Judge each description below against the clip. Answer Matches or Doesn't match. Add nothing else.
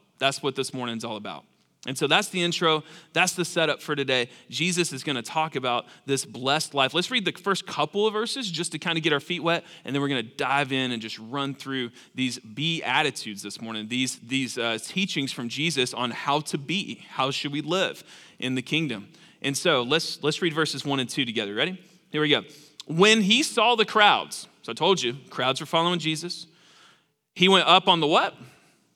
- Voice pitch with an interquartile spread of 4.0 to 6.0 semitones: Matches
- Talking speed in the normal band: Doesn't match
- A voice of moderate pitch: Matches